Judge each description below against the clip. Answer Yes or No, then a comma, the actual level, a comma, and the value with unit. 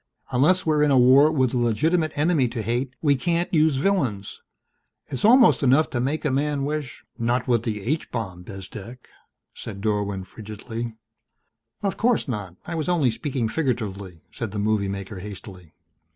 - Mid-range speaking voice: No, low, 125 Hz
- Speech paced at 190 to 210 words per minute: No, average, 170 wpm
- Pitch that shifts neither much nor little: No, wide, 6.2 semitones